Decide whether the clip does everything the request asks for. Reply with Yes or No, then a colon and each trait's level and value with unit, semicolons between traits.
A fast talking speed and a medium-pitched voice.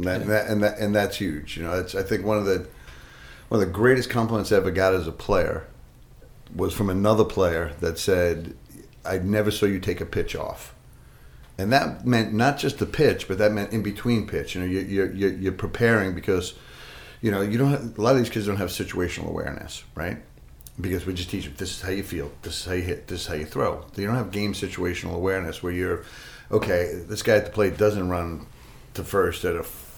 No: fast, 235 wpm; very low, 95 Hz